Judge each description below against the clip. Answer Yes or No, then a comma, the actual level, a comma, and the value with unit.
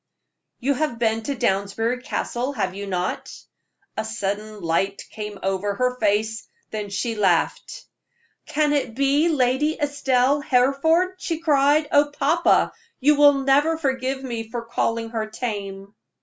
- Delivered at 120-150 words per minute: Yes, average, 140 wpm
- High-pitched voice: Yes, very high, 250 Hz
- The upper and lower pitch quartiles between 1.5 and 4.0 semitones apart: No, average, 5.3 semitones